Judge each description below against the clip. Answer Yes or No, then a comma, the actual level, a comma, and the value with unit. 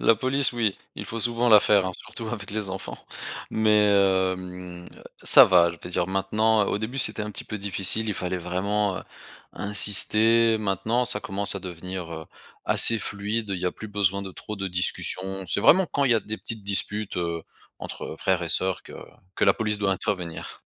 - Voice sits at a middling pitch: No, low, 100 Hz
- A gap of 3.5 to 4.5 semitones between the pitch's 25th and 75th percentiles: No, average, 2.8 semitones